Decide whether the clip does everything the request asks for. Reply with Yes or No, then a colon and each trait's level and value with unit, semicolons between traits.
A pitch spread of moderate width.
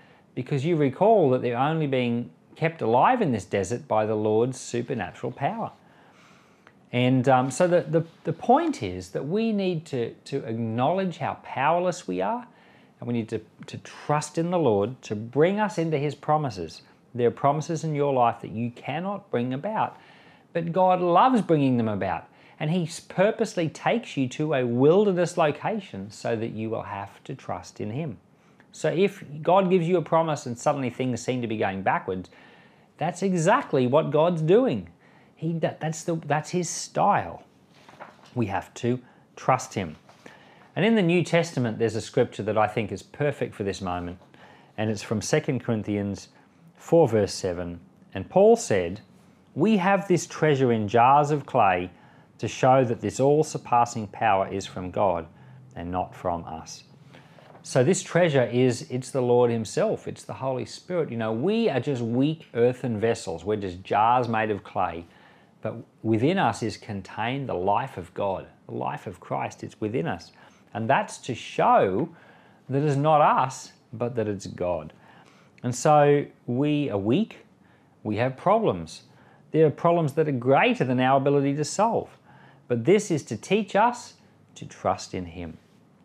No: wide, 6.2 semitones